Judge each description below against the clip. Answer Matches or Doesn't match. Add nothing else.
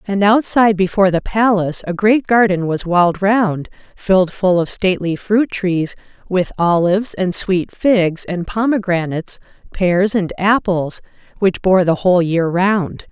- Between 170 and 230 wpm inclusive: Doesn't match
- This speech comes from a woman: Matches